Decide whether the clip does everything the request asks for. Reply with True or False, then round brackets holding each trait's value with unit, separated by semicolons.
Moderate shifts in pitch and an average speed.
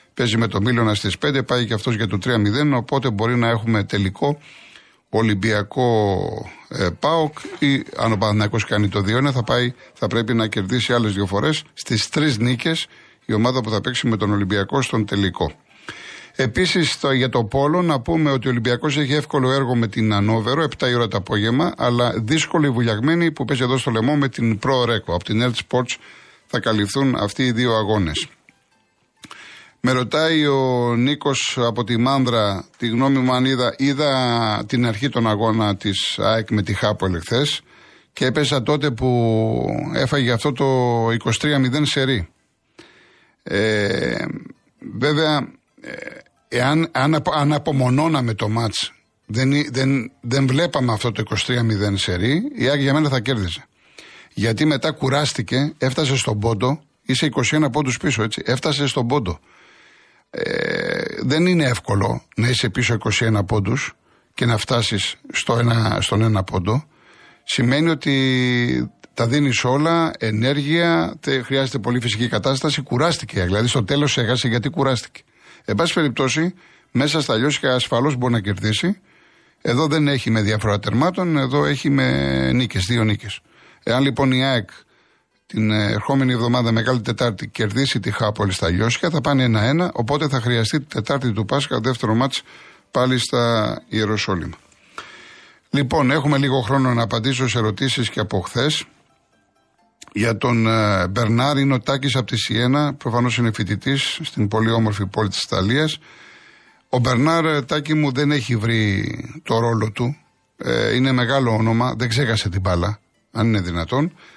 True (4.1 semitones; 155 wpm)